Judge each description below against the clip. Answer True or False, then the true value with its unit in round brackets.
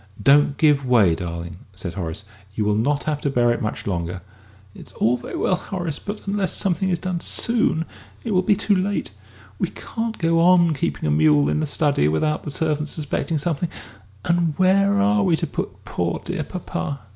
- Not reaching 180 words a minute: False (190 wpm)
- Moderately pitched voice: True (150 Hz)